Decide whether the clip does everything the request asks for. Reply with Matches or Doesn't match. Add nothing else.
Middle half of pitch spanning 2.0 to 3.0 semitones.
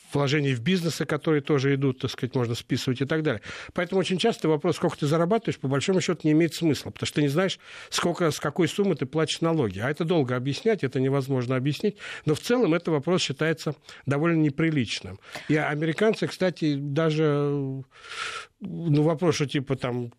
Doesn't match